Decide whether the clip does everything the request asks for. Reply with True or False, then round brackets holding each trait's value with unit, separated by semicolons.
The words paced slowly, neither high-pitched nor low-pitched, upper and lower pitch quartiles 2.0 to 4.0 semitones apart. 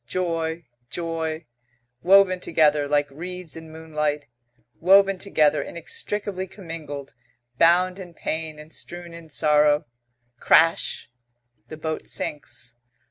True (105 wpm; 160 Hz; 2.9 semitones)